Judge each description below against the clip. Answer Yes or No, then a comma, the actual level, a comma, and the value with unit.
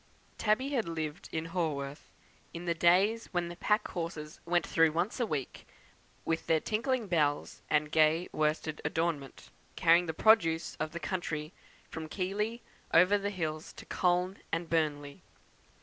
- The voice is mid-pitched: Yes, medium, 170 Hz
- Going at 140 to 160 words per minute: Yes, average, 150 wpm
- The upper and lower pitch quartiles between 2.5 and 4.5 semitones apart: Yes, average, 3.2 semitones